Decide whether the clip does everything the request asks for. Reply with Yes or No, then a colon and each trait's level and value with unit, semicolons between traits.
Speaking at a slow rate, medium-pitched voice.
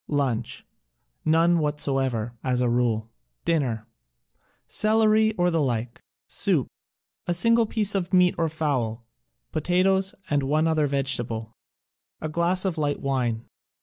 Yes: slow, 125 wpm; medium, 150 Hz